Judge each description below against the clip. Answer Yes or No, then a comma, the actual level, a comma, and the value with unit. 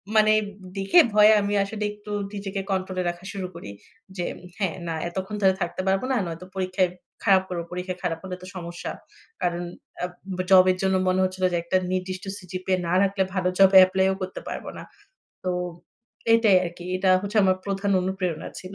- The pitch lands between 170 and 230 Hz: Yes, medium, 185 Hz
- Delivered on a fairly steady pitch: Yes, narrow, 1.2 semitones